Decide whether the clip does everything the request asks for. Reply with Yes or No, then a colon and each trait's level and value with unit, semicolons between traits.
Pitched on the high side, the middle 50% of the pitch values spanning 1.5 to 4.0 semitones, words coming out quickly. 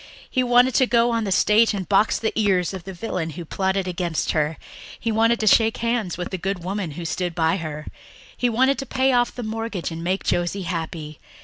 No: high, 195 Hz; average, 4.8 semitones; fast, 220 wpm